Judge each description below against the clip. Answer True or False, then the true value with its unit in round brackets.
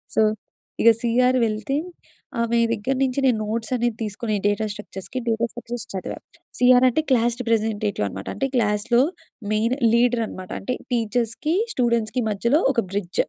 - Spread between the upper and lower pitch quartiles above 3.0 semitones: False (2.4 semitones)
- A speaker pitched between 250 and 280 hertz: False (230 Hz)